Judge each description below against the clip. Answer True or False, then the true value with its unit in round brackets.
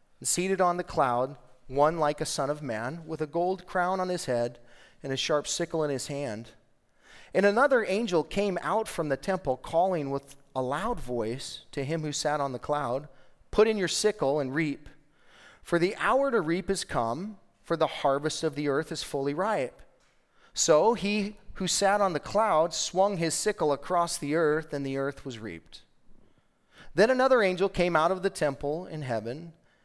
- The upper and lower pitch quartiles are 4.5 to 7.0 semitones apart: True (5.2 semitones)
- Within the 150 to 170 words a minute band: False (190 wpm)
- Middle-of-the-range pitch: True (155 Hz)